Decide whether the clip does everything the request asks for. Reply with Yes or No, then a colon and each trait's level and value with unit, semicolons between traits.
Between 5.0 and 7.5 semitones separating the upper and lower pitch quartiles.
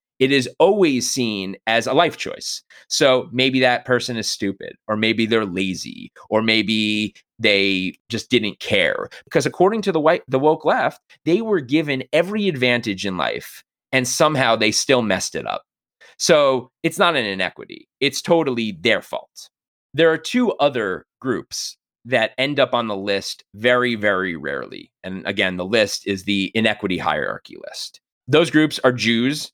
Yes: wide, 5.6 semitones